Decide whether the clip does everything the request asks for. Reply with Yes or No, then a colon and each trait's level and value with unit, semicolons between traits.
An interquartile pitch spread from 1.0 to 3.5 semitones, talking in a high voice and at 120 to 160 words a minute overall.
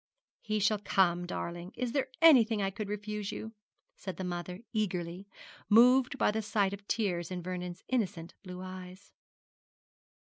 Yes: average, 3.1 semitones; high, 200 Hz; average, 150 wpm